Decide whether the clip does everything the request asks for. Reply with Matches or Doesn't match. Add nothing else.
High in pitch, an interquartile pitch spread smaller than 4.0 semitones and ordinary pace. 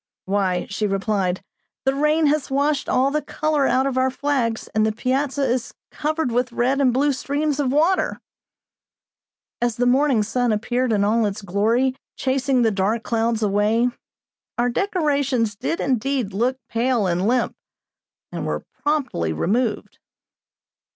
Doesn't match